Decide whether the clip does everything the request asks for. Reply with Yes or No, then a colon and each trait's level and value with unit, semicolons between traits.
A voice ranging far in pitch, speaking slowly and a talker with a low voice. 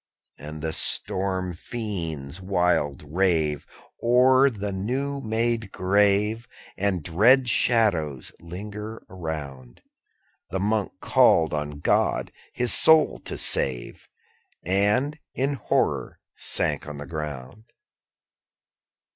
Yes: wide, 6.3 semitones; slow, 105 wpm; very low, 95 Hz